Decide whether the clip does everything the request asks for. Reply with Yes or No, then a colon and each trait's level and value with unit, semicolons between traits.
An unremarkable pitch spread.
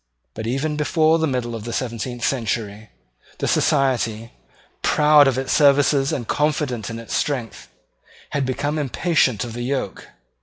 Yes: average, 4.0 semitones